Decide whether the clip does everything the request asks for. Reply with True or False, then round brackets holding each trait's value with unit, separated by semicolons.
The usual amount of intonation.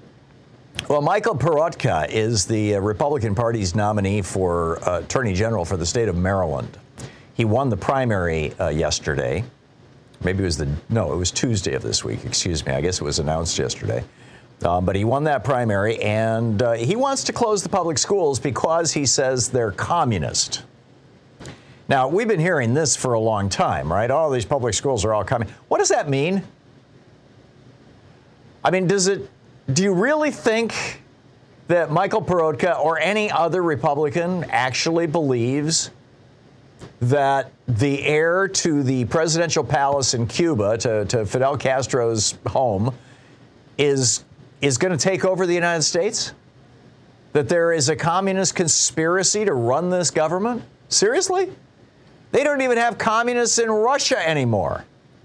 False (6.9 semitones)